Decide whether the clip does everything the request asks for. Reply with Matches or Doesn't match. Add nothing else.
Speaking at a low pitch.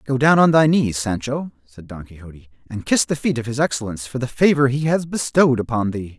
Matches